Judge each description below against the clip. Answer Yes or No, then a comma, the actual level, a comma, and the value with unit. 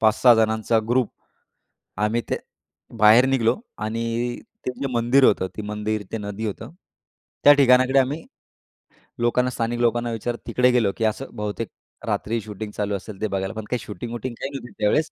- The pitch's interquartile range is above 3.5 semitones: No, narrow, 2.5 semitones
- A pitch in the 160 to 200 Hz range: No, low, 115 Hz